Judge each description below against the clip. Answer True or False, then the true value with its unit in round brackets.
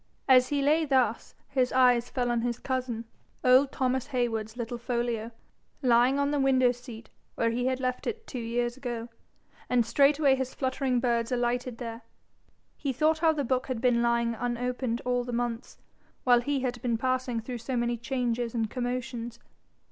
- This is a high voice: True (245 Hz)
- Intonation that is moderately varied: False (1.7 semitones)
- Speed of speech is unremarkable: True (175 wpm)